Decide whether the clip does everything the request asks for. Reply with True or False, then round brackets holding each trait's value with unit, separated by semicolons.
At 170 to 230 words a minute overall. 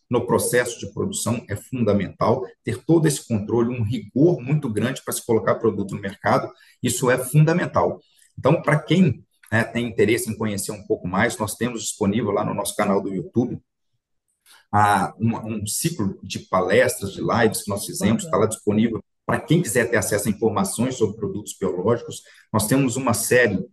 True (175 wpm)